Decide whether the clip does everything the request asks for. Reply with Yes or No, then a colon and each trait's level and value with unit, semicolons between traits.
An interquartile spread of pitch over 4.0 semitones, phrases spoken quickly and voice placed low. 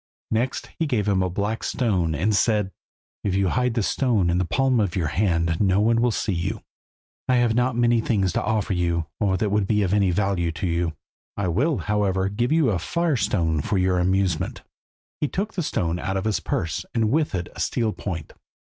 Yes: average, 4.4 semitones; fast, 215 wpm; low, 100 Hz